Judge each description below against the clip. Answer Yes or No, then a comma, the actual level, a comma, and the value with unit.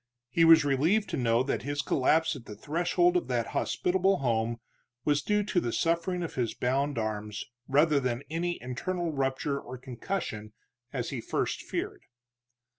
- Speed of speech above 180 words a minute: No, average, 170 wpm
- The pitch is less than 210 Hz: Yes, medium, 140 Hz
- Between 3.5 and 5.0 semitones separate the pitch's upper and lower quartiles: No, wide, 5.5 semitones